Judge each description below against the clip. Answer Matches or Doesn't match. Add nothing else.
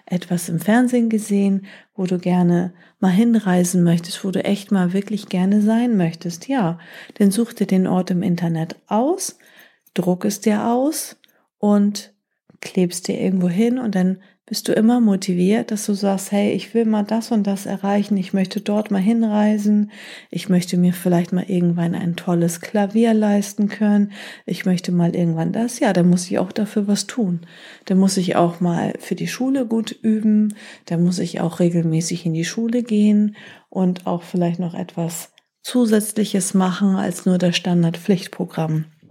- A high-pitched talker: Matches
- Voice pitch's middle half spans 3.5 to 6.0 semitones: Doesn't match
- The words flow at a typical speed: Matches